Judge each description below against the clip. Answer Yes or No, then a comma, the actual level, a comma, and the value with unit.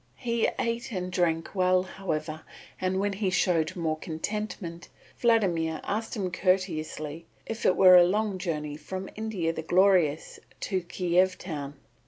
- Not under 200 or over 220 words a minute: No, average, 145 wpm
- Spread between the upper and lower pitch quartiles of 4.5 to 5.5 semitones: No, average, 3.3 semitones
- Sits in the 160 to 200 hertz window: Yes, medium, 185 Hz